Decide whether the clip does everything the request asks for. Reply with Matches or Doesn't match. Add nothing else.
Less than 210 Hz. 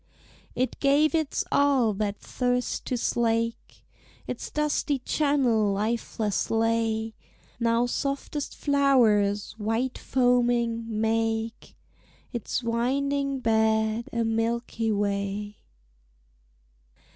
Doesn't match